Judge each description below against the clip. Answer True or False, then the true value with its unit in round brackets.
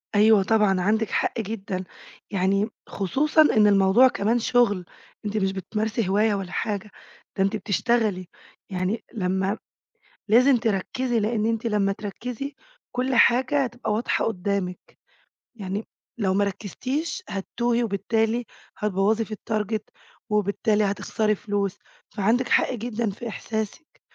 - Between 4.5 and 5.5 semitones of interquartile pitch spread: False (2.9 semitones)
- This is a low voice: False (215 Hz)